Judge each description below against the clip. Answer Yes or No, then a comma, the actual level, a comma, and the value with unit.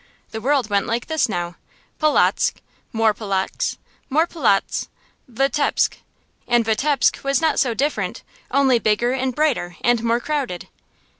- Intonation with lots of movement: No, average, 4.1 semitones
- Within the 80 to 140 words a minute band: Yes, slow, 135 wpm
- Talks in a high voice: Yes, high, 240 Hz